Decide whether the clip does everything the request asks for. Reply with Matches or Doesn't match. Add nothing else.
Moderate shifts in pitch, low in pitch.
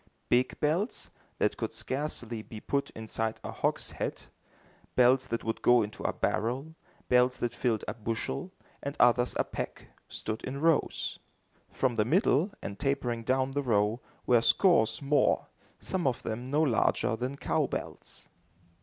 Matches